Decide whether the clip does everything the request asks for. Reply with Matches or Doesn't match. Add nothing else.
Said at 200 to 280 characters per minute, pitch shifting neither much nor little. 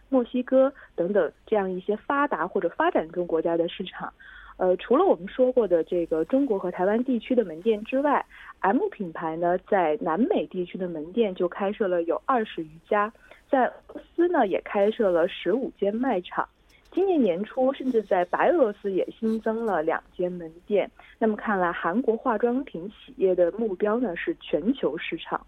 Doesn't match